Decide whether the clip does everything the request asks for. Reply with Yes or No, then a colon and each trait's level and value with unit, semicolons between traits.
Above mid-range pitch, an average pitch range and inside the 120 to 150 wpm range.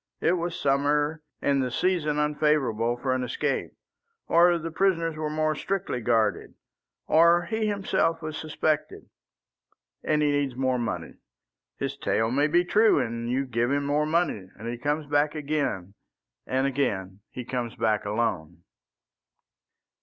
No: medium, 145 Hz; average, 4.6 semitones; average, 145 wpm